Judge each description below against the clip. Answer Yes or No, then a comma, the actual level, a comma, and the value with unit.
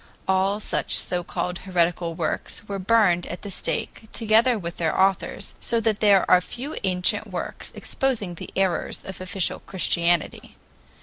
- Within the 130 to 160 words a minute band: Yes, average, 150 wpm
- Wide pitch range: No, average, 3.3 semitones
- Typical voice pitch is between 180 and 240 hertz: Yes, high, 190 Hz